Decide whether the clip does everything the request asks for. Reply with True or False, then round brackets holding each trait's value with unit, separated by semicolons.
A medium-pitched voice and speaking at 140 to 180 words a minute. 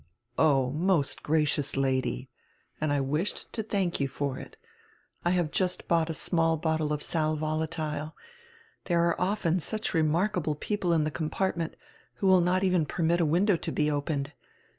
True (160 Hz; 170 wpm)